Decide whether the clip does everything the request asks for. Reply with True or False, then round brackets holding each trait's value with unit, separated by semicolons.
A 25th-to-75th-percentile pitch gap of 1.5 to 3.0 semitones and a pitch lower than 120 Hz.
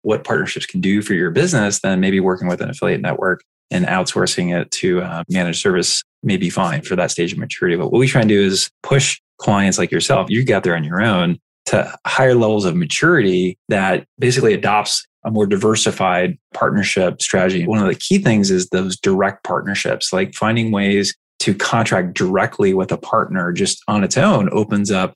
True (2.7 semitones; 100 Hz)